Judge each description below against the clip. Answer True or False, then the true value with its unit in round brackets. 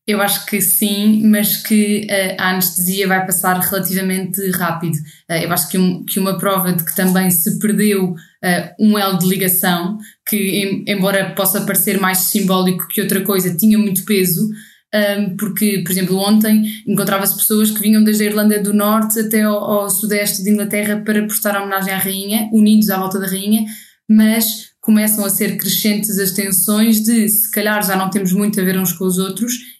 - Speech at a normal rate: False (190 wpm)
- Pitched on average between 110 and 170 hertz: False (200 Hz)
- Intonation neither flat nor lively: False (1.9 semitones)